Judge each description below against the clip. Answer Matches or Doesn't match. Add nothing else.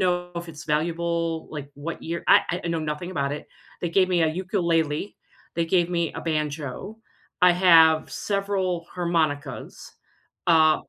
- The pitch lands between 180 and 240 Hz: Doesn't match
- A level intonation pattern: Matches